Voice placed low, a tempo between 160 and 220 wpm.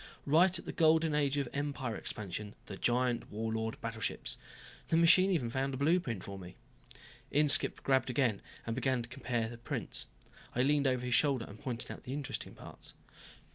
Yes: low, 130 Hz; average, 175 wpm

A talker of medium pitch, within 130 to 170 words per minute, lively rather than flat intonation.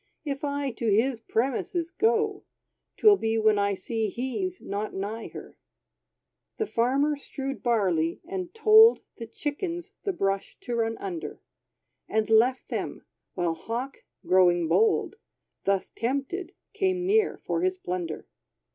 No: very high, 260 Hz; slow, 135 wpm; wide, 9.0 semitones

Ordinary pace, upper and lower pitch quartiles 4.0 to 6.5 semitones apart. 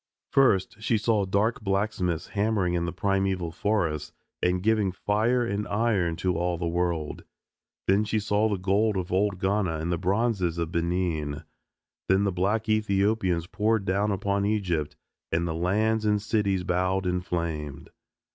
No: average, 155 wpm; average, 3.2 semitones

